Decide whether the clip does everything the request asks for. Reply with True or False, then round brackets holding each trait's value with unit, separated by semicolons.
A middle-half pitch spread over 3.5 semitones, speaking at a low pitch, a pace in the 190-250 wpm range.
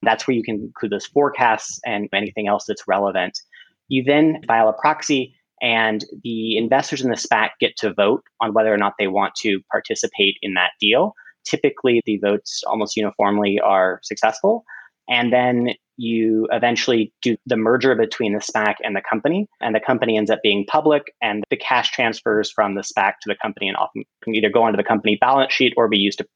True (3.9 semitones; 115 Hz; 200 wpm)